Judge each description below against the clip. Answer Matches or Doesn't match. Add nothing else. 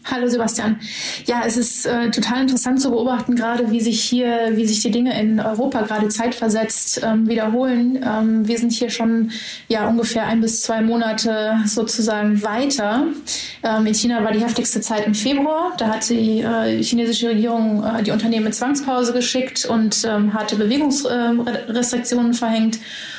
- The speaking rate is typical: Matches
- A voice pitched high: Matches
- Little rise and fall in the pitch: Matches